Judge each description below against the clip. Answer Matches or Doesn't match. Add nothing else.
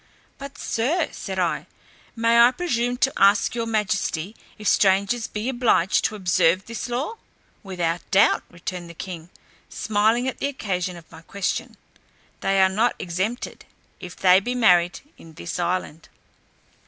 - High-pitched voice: Matches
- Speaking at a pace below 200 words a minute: Matches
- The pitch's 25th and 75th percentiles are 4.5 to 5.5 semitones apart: Matches